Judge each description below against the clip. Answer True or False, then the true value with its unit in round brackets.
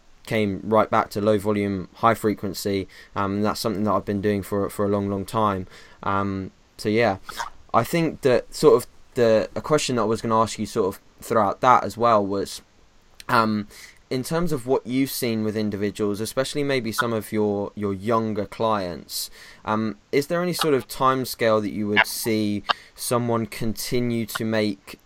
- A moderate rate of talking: True (190 wpm)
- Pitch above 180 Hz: False (110 Hz)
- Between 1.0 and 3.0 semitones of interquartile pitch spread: True (2.5 semitones)